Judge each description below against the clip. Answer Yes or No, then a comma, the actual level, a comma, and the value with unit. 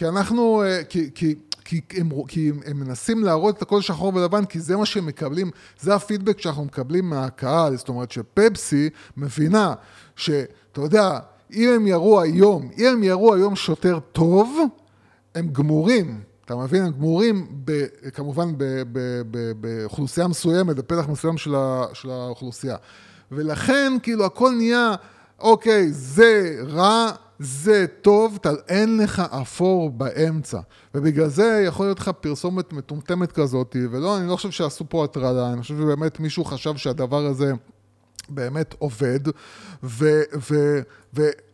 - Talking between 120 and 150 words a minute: Yes, average, 125 wpm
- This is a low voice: No, medium, 160 Hz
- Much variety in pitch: Yes, wide, 6.1 semitones